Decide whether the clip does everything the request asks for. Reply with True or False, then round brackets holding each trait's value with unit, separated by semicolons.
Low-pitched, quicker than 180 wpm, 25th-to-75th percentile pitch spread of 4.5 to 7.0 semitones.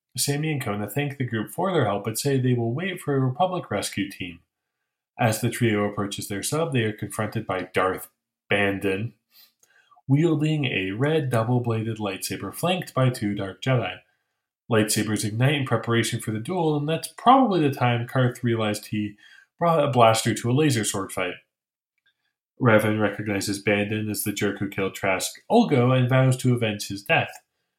False (115 Hz; 175 wpm; 5.4 semitones)